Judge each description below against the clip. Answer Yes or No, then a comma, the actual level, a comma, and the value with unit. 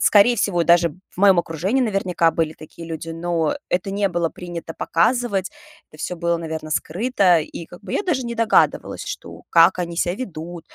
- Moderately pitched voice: Yes, medium, 175 Hz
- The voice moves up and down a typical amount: Yes, average, 3.3 semitones